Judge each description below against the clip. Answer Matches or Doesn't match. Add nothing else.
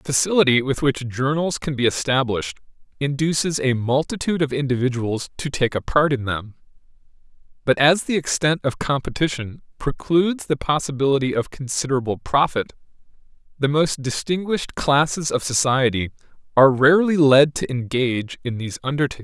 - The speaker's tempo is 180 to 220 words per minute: Doesn't match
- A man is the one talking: Matches